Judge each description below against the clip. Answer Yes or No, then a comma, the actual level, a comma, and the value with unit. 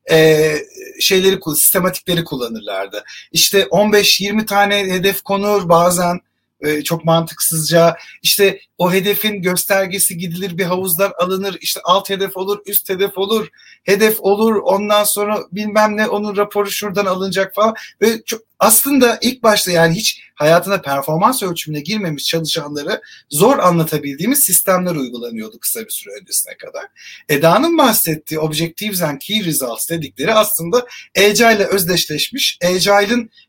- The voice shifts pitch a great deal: No, average, 3.8 semitones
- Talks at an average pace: Yes, average, 125 wpm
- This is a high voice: Yes, high, 195 Hz